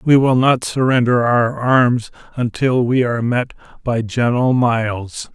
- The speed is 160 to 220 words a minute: No, average, 145 wpm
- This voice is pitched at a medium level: No, low, 120 Hz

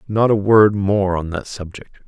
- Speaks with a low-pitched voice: Yes, low, 100 Hz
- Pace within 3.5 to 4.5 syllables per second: Yes, 4.4 syllables/s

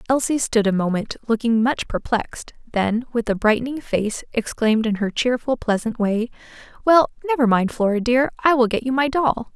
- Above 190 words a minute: No, average, 180 wpm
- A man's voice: No, female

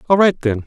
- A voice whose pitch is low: No, medium, 145 Hz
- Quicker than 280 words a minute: No, fast, 270 wpm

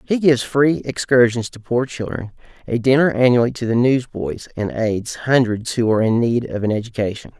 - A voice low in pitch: Yes, low, 120 Hz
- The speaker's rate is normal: Yes, average, 185 wpm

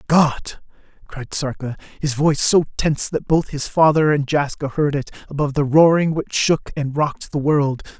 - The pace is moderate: Yes, average, 180 wpm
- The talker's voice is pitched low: No, medium, 145 Hz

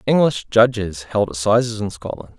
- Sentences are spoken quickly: No, average, 150 wpm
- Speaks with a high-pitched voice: No, low, 110 Hz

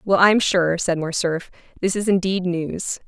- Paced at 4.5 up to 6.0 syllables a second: No, 4.2 syllables/s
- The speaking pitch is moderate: Yes, medium, 180 Hz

